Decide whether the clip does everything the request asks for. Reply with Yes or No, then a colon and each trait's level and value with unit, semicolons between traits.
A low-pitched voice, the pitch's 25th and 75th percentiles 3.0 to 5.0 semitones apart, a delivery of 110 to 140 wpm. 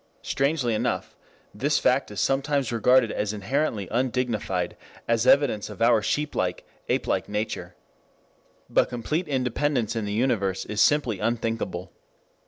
Yes: low, 115 Hz; average, 4.2 semitones; slow, 135 wpm